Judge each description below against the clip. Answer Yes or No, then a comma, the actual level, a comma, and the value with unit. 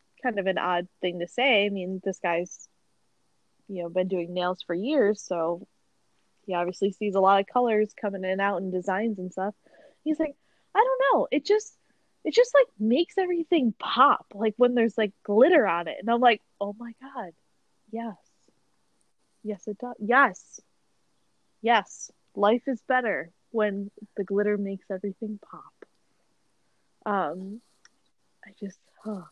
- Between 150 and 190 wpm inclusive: Yes, average, 160 wpm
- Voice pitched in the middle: No, high, 210 Hz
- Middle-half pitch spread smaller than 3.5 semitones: No, average, 4.3 semitones